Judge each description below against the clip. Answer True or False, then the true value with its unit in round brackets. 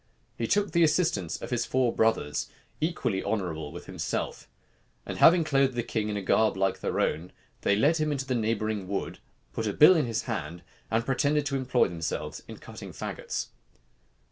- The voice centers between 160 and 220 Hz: False (115 Hz)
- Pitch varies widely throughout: True (6.3 semitones)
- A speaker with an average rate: True (185 wpm)